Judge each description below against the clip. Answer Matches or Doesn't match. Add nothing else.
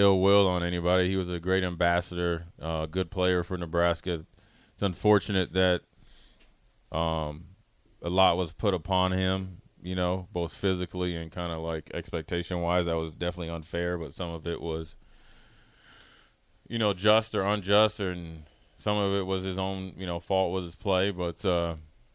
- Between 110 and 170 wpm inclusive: Matches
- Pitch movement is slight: Matches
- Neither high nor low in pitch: Doesn't match